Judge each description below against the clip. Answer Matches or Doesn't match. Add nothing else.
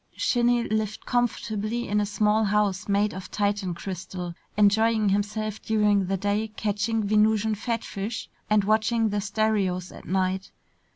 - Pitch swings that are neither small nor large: Doesn't match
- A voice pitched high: Matches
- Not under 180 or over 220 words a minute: Doesn't match